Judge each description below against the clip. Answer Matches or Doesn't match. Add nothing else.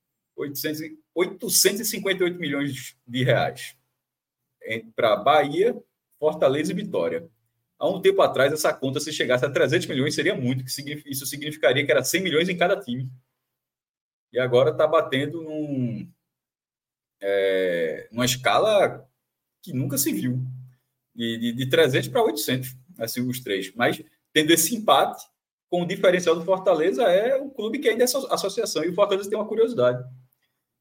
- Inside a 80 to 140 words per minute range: Doesn't match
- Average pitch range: Doesn't match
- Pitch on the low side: Doesn't match